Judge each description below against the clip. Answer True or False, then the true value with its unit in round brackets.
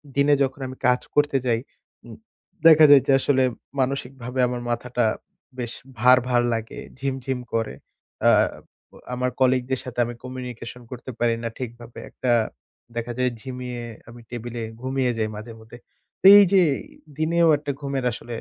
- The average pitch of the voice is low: True (125 Hz)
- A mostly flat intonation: True (1.8 semitones)